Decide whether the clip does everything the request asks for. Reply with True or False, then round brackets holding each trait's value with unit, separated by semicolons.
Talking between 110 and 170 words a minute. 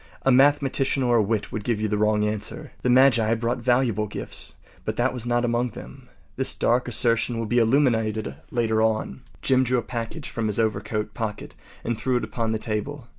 False (200 wpm)